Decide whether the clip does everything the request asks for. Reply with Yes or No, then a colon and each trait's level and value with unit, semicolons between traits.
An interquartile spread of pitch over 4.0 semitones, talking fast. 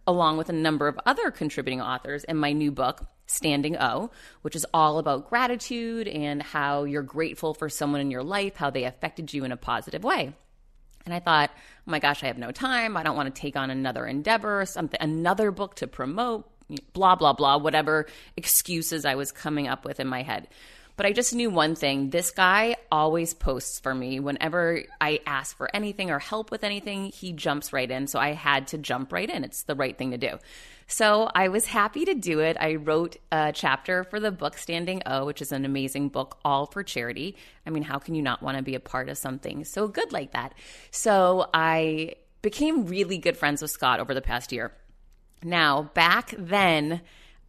Yes: average, 4.8 semitones; fast, 210 wpm